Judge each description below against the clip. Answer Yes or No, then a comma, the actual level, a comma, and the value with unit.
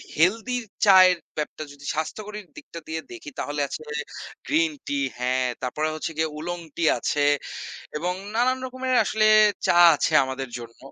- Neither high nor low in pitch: Yes, medium, 165 Hz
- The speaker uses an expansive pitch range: Yes, wide, 6.9 semitones